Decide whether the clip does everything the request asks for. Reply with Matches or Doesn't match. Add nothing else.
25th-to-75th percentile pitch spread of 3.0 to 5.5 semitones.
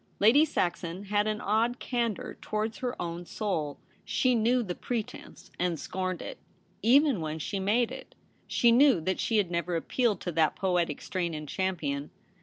Matches